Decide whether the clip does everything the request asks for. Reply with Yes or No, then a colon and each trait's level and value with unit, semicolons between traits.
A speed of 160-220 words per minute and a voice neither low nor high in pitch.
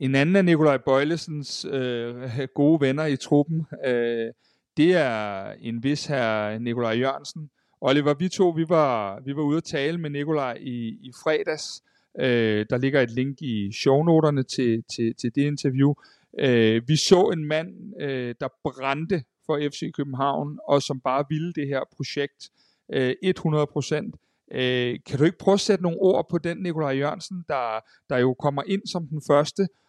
Yes: average, 175 wpm; medium, 145 Hz